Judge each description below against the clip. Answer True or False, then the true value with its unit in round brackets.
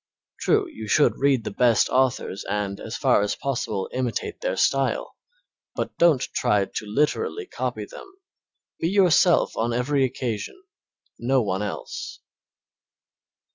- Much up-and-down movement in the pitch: True (5.8 semitones)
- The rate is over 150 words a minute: False (135 wpm)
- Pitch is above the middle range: False (125 Hz)